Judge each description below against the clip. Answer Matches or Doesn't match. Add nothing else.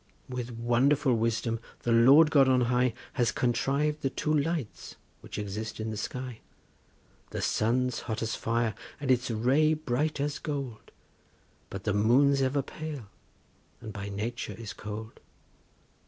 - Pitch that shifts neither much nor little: Matches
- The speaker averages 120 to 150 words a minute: Matches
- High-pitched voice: Doesn't match